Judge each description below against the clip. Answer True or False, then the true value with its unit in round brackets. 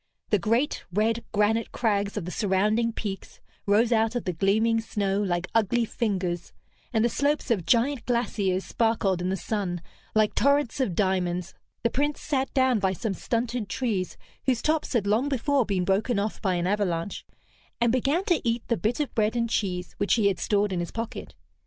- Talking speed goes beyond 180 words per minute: True (190 wpm)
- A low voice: False (220 Hz)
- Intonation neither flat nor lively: True (3.6 semitones)